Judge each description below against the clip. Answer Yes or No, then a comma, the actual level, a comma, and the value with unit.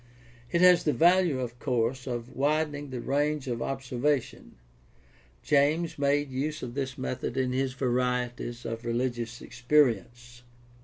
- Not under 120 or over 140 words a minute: Yes, slow, 135 wpm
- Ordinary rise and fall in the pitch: Yes, average, 3.3 semitones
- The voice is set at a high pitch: No, low, 130 Hz